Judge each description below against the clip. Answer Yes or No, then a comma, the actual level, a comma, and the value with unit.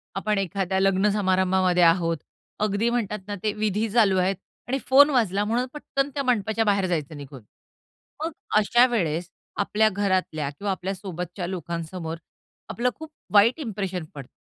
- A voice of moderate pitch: No, high, 195 Hz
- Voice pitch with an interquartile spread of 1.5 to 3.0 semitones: No, average, 3.4 semitones